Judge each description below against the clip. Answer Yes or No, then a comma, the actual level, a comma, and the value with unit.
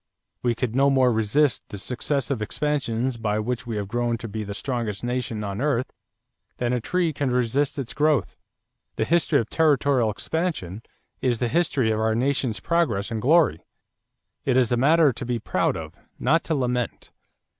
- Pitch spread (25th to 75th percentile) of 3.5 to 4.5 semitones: Yes, average, 4.1 semitones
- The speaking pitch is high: No, low, 125 Hz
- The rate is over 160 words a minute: Yes, average, 175 wpm